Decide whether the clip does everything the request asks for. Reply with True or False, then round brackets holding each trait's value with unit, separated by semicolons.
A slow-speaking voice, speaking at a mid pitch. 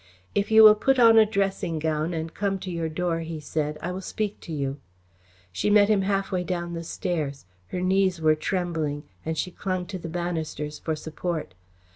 False (195 wpm; 175 Hz)